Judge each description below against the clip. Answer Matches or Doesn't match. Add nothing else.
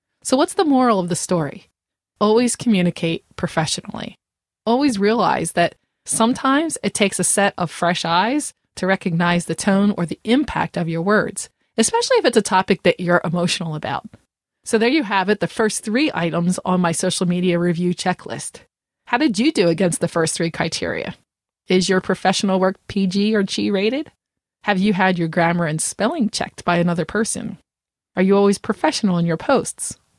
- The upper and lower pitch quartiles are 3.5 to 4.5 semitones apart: Matches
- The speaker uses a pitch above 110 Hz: Matches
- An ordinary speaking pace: Matches